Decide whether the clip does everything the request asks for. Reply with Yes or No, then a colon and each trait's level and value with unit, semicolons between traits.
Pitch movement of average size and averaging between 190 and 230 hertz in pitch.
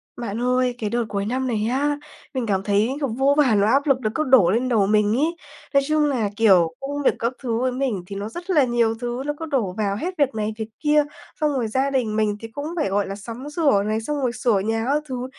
No: average, 4.5 semitones; high, 240 Hz